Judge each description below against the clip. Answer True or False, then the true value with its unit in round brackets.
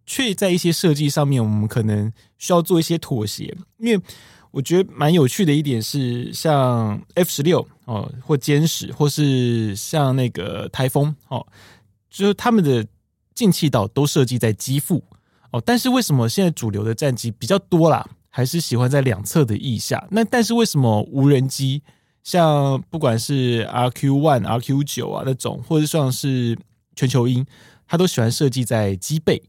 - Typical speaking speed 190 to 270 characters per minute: True (260 characters per minute)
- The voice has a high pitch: False (135 Hz)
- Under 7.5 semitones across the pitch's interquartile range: True (5.6 semitones)